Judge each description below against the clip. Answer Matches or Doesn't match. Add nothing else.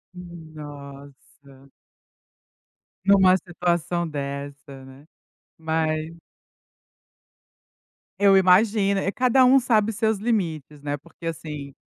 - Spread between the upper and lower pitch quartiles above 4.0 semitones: Matches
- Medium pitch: Matches